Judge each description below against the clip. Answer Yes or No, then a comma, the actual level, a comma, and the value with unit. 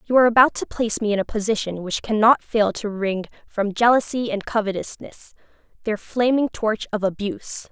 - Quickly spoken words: No, average, 180 wpm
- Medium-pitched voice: No, high, 215 Hz